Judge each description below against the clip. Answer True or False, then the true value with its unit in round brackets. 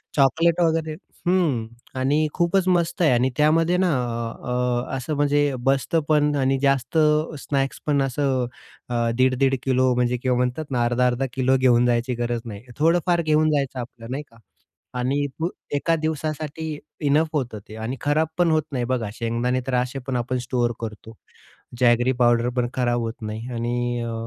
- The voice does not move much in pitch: False (3.8 semitones)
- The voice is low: True (130 Hz)